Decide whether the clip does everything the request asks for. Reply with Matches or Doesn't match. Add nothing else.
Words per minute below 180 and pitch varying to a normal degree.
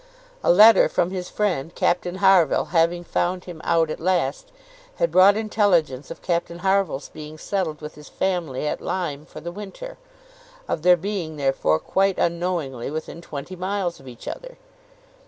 Matches